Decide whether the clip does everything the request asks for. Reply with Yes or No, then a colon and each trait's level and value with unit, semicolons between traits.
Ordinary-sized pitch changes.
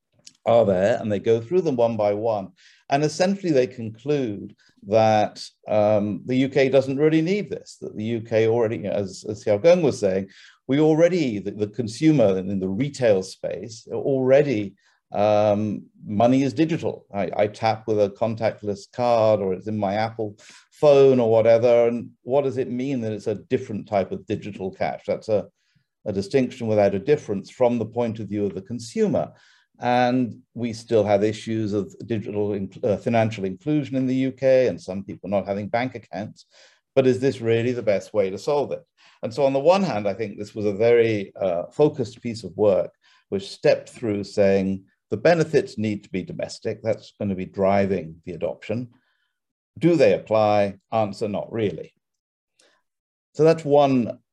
Yes: average, 4.3 semitones